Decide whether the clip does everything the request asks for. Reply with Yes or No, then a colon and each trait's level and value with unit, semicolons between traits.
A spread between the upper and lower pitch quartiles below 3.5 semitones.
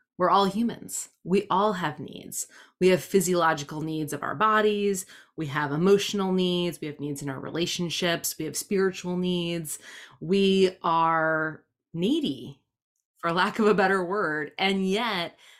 No: average, 3.8 semitones